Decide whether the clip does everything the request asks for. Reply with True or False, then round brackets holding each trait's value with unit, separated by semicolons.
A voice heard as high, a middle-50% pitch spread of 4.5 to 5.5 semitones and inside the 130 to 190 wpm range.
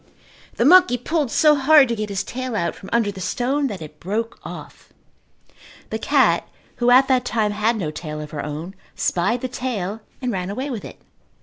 False (230 Hz; 5.2 semitones; 200 wpm)